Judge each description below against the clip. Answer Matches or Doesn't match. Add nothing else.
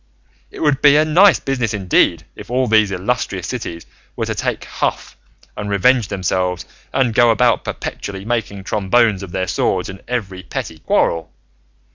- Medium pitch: Doesn't match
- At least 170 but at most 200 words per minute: Doesn't match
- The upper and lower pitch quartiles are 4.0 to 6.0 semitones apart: Matches